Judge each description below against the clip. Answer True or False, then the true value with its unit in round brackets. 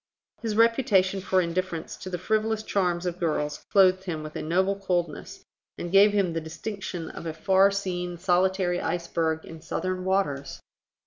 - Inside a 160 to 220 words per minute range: True (165 wpm)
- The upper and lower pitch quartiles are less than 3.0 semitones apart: True (2.6 semitones)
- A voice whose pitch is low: False (185 Hz)